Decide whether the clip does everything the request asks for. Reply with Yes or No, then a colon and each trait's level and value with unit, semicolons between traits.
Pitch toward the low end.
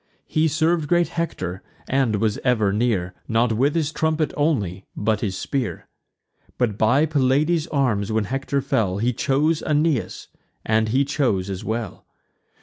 Yes: low, 125 Hz